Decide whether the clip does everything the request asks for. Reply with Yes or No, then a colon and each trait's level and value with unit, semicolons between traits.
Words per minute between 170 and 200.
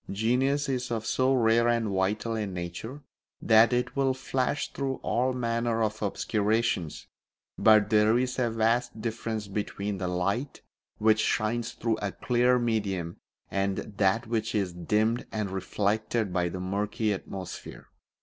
No: average, 145 wpm